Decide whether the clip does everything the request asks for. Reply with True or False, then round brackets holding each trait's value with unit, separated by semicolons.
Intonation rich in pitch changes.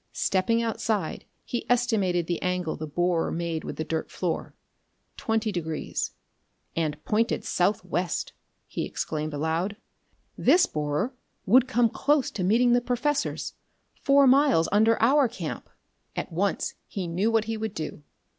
True (6.0 semitones)